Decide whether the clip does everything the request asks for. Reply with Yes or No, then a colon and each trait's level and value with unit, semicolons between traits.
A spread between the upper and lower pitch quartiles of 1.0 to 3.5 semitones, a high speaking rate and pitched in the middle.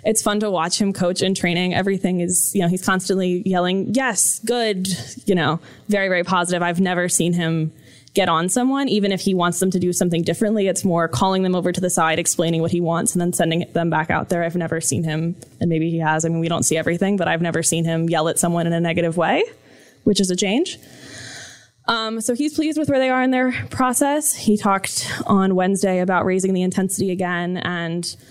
Yes: average, 2.9 semitones; fast, 230 wpm; medium, 180 Hz